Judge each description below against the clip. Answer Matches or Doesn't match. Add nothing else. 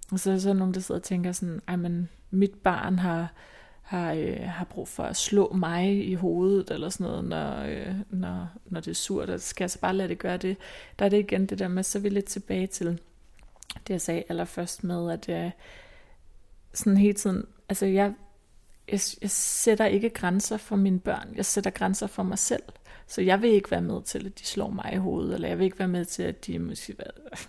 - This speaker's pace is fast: Matches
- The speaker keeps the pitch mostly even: Matches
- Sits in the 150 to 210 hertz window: Matches